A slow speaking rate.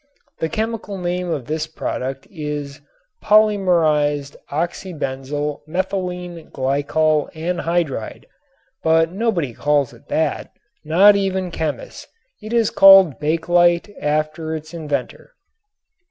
Yes: slow, 100 wpm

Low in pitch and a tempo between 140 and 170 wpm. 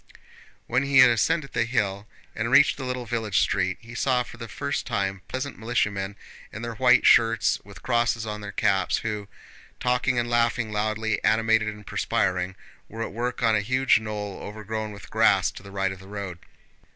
No: low, 110 Hz; average, 190 wpm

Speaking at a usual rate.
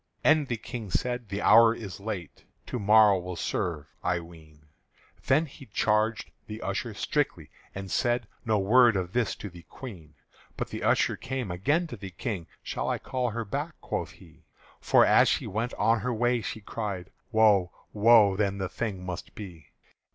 Yes: average, 180 wpm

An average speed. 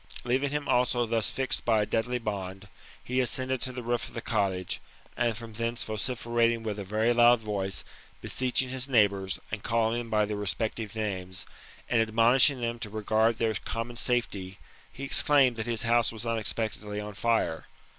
Yes: average, 180 wpm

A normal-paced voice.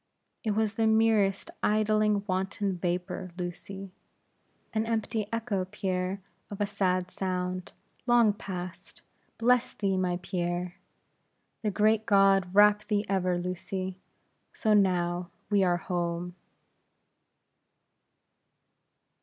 No: slow, 105 wpm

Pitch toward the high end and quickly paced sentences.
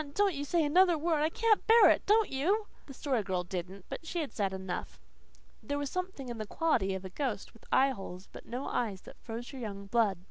Yes: very high, 260 Hz; fast, 225 wpm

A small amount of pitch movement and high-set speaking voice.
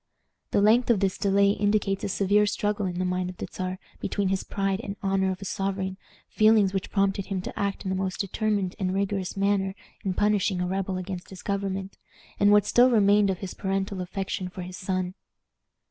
Yes: narrow, 1.3 semitones; high, 195 Hz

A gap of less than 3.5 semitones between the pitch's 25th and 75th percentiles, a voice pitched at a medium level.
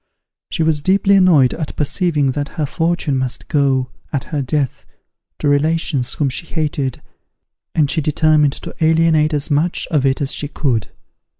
Yes: average, 2.7 semitones; medium, 150 Hz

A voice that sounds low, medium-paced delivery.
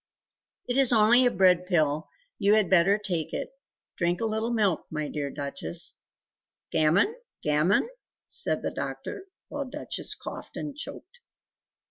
No: high, 195 Hz; average, 145 wpm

